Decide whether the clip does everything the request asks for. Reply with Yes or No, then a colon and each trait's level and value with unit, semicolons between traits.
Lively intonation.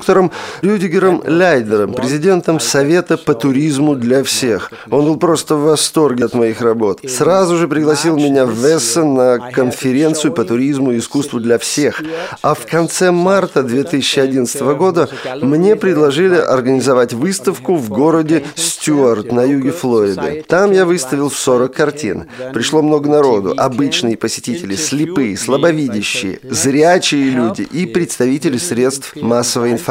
No: average, 4.4 semitones